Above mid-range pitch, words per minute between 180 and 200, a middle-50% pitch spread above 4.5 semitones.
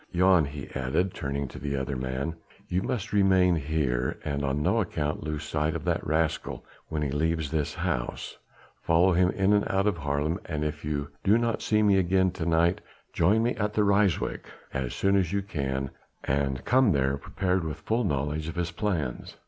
No: very low, 80 Hz; average, 190 wpm; average, 5.0 semitones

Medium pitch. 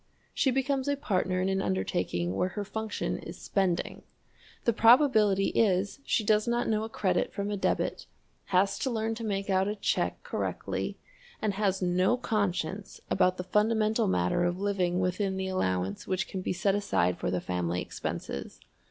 No: high, 195 Hz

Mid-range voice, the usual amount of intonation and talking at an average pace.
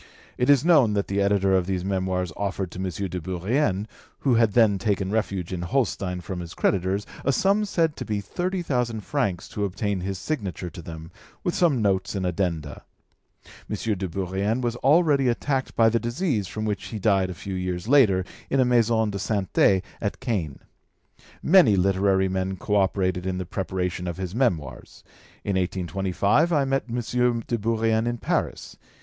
No: low, 100 Hz; average, 4.2 semitones; average, 180 wpm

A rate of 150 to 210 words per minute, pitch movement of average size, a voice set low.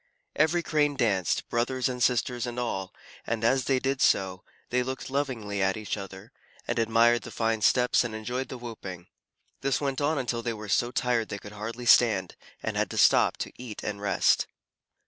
Yes: average, 190 wpm; average, 3.4 semitones; low, 120 Hz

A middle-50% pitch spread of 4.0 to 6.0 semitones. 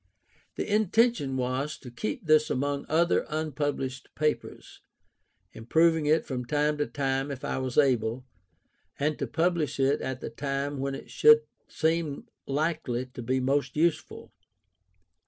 No: average, 3.2 semitones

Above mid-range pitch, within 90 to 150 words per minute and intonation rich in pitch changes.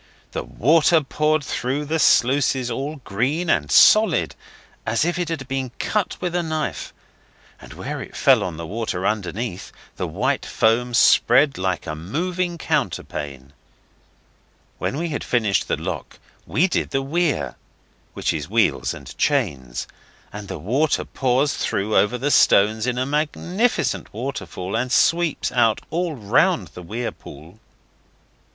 No: low, 130 Hz; average, 145 wpm; wide, 6.9 semitones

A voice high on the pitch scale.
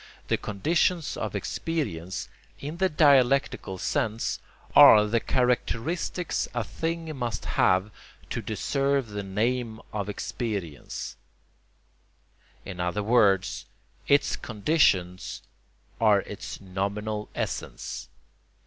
No: low, 110 Hz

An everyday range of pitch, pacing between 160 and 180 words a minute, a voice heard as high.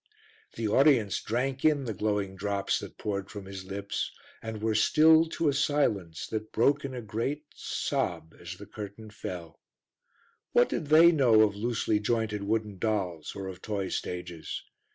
No: average, 4.2 semitones; average, 165 wpm; low, 110 Hz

